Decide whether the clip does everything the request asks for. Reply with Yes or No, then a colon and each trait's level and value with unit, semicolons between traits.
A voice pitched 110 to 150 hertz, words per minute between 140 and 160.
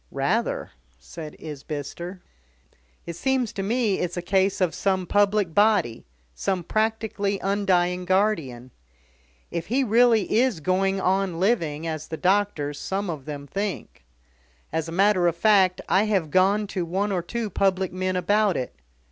No: high, 190 Hz; average, 150 wpm